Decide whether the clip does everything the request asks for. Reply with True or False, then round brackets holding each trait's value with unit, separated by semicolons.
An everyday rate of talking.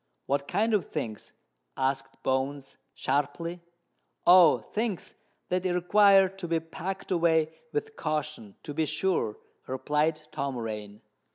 False (120 wpm)